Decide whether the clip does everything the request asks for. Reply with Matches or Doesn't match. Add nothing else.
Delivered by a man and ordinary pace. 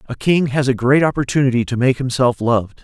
Doesn't match